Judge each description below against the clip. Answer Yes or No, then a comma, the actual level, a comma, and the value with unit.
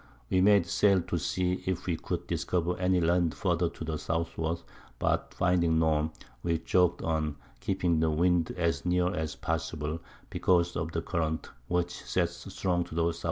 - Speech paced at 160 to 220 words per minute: Yes, average, 170 wpm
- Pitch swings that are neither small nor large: No, narrow, 1.7 semitones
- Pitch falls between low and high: No, very low, 85 Hz